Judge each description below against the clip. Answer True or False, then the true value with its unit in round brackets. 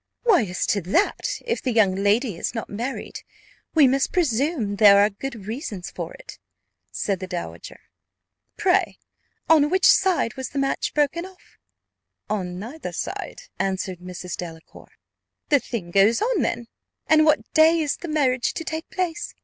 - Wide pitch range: True (8.1 semitones)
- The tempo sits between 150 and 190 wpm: True (160 wpm)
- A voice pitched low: False (255 Hz)